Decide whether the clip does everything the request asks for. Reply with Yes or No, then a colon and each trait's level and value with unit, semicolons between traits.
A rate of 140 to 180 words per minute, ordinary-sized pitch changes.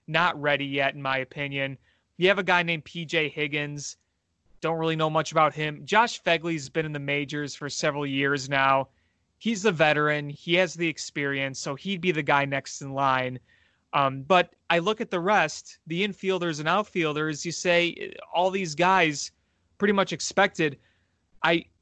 Yes: average, 175 wpm; average, 4.1 semitones